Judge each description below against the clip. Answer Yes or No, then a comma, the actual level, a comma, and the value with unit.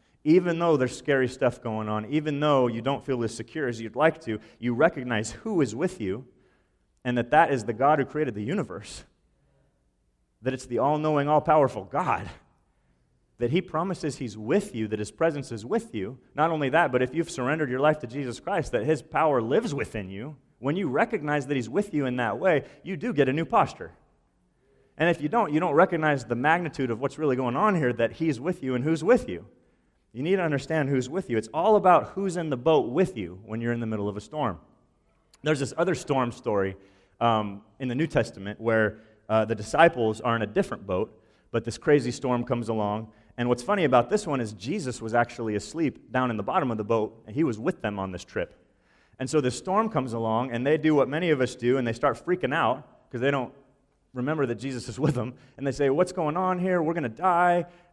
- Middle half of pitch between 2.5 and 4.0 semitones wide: No, average, 5.2 semitones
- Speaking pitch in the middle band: No, low, 130 Hz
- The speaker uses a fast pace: Yes, fast, 235 wpm